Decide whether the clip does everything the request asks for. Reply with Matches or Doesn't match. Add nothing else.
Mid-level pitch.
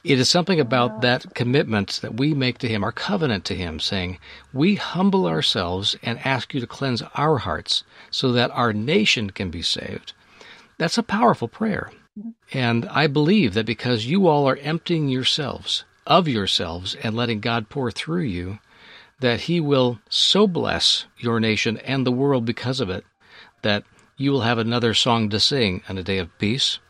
Doesn't match